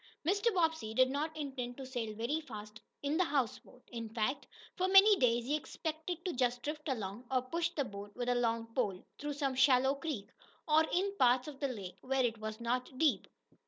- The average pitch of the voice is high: Yes, very high, 260 Hz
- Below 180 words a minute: No, average, 200 wpm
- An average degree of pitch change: Yes, average, 4.7 semitones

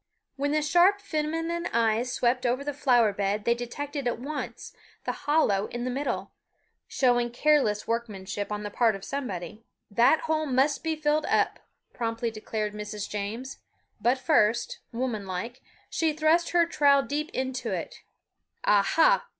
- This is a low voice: No, very high, 250 Hz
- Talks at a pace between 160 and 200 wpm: No, average, 150 wpm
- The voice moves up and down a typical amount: No, wide, 5.8 semitones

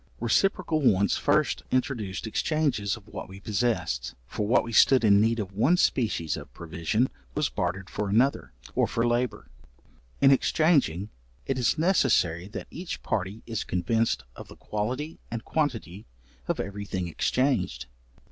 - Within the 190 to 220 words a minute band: No, average, 150 wpm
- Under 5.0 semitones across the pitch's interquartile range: No, average, 5.3 semitones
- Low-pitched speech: Yes, low, 110 Hz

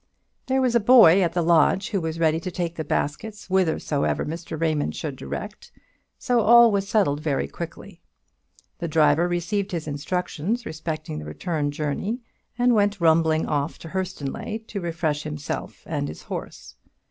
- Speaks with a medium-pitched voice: Yes, medium, 165 Hz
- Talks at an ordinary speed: Yes, average, 160 wpm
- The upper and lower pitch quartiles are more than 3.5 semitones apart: Yes, average, 4.8 semitones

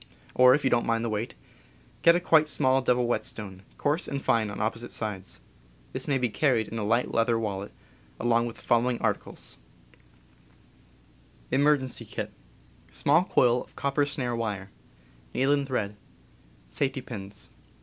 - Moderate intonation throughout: Yes, average, 3.5 semitones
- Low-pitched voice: Yes, low, 120 Hz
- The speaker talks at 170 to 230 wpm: No, average, 150 wpm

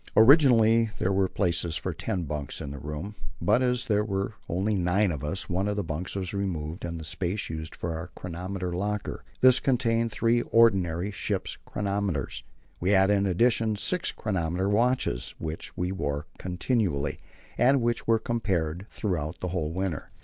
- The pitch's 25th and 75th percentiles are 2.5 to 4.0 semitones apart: No, average, 4.5 semitones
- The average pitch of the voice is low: Yes, very low, 95 Hz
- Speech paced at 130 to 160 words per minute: No, average, 170 wpm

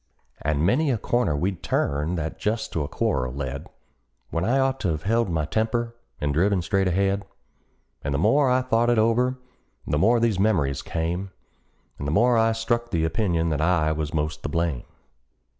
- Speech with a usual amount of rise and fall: No, wide, 6.7 semitones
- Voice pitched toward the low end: Yes, very low, 95 Hz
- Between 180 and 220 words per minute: Yes, average, 190 wpm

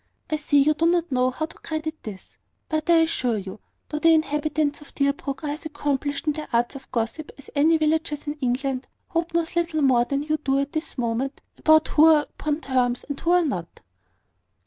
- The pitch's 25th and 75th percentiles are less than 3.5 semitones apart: Yes, average, 2.7 semitones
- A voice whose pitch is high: Yes, very high, 295 Hz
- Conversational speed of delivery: No, fast, 210 wpm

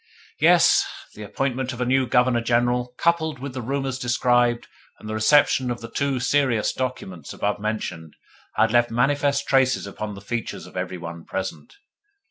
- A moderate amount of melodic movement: Yes, average, 3.5 semitones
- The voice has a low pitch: Yes, low, 120 Hz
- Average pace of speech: Yes, average, 165 wpm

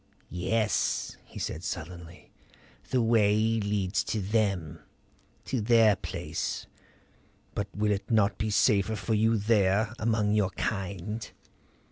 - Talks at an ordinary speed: No, slow, 120 wpm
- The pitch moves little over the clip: Yes, narrow, 2.3 semitones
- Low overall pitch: Yes, low, 105 Hz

